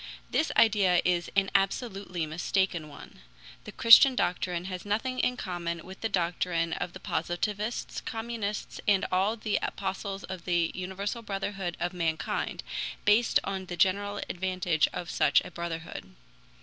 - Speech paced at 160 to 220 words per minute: No, average, 145 wpm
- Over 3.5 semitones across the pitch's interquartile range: No, average, 2.8 semitones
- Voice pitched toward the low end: No, high, 190 Hz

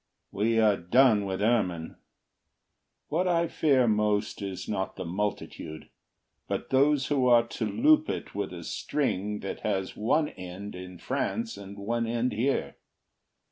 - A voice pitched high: No, low, 110 Hz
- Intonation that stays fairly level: No, average, 5.1 semitones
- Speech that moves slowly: No, average, 145 wpm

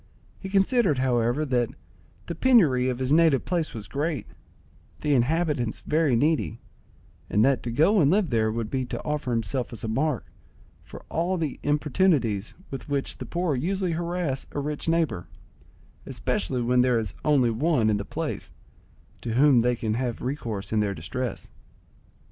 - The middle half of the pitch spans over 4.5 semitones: Yes, average, 5.3 semitones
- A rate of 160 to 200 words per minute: Yes, average, 165 wpm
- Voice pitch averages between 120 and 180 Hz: Yes, low, 135 Hz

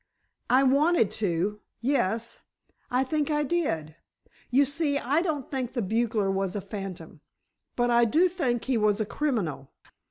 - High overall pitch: Yes, high, 240 Hz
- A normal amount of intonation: No, wide, 5.8 semitones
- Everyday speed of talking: Yes, average, 150 wpm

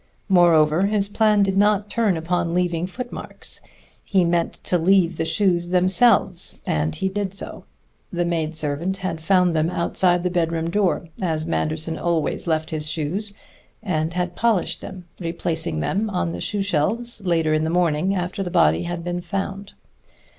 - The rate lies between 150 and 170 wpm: Yes, average, 160 wpm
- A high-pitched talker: No, medium, 175 Hz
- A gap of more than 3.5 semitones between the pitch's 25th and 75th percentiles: No, average, 3.0 semitones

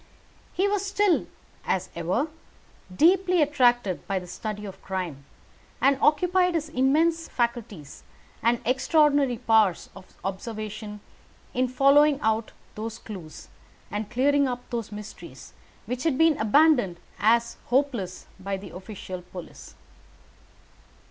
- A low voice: No, high, 235 Hz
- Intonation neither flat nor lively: No, wide, 6.7 semitones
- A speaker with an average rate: No, slow, 120 wpm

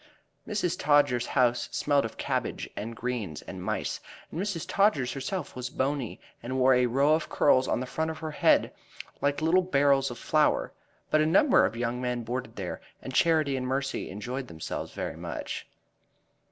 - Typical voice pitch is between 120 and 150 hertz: Yes, low, 135 Hz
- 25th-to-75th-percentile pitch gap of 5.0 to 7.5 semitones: No, average, 3.9 semitones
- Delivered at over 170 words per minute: Yes, average, 180 wpm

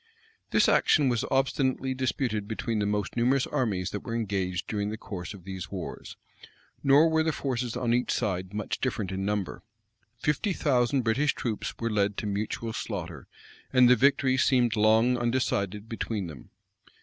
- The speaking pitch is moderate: No, low, 115 Hz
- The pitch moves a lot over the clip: No, average, 4.2 semitones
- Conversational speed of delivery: Yes, average, 170 wpm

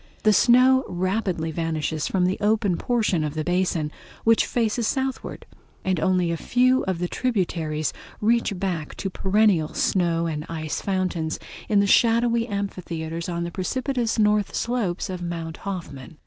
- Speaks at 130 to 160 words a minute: Yes, average, 150 wpm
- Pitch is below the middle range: No, medium, 185 Hz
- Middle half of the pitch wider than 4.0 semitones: Yes, average, 4.8 semitones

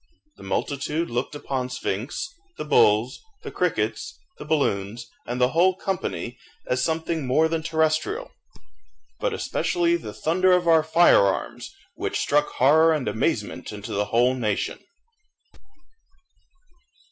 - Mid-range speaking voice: Yes, medium, 150 Hz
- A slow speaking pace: Yes, slow, 130 wpm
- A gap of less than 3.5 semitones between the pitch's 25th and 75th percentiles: No, average, 5.0 semitones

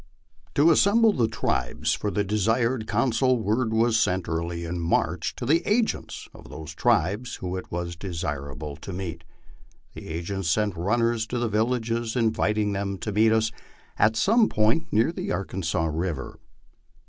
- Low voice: Yes, low, 105 Hz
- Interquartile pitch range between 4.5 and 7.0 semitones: Yes, average, 5.1 semitones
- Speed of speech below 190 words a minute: Yes, average, 160 wpm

